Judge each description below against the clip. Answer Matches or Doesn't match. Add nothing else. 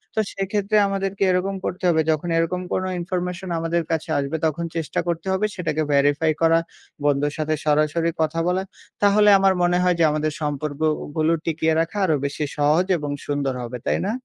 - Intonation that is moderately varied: Matches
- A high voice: Doesn't match